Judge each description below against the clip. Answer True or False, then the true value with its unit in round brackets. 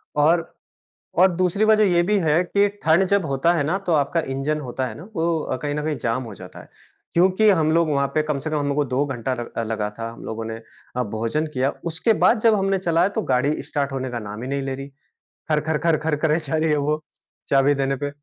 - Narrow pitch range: False (3.9 semitones)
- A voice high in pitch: False (150 Hz)